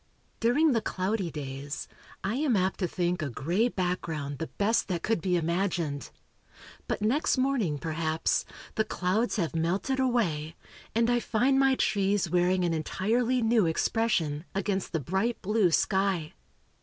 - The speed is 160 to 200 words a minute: No, average, 150 wpm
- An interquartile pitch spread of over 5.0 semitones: Yes, wide, 5.6 semitones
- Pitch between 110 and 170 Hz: No, high, 190 Hz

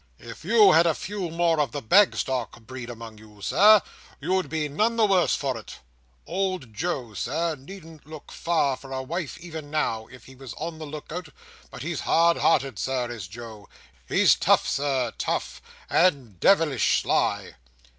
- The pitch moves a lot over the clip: Yes, wide, 5.8 semitones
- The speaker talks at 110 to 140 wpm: No, average, 175 wpm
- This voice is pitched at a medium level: Yes, medium, 145 Hz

